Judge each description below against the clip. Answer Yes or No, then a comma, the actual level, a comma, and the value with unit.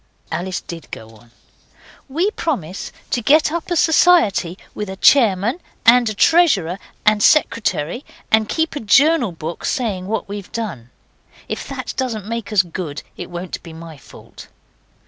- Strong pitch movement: Yes, wide, 7.1 semitones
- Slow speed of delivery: No, average, 155 wpm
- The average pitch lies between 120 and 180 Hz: No, high, 210 Hz